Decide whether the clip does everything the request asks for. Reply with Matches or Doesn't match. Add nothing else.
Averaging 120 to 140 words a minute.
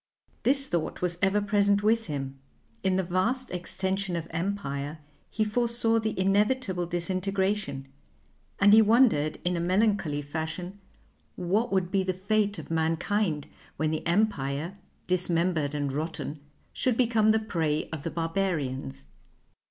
Matches